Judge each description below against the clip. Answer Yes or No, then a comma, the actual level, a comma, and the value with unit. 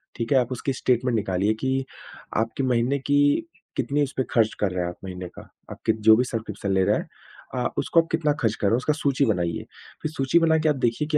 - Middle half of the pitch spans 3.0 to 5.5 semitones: Yes, average, 4.8 semitones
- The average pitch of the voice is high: No, low, 125 Hz